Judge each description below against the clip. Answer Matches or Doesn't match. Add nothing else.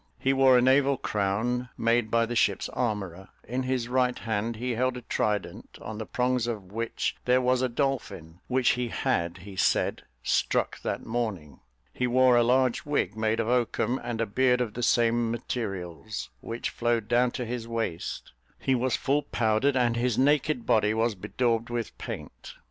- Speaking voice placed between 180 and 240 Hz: Doesn't match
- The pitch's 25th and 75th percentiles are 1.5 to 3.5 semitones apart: Matches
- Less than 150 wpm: Doesn't match